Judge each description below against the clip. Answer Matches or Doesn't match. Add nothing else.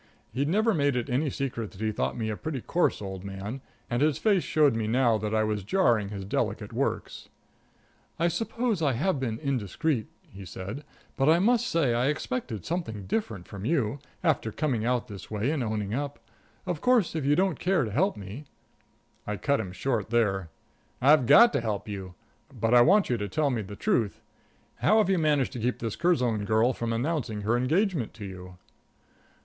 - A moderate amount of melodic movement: Doesn't match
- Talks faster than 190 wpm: Matches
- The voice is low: Matches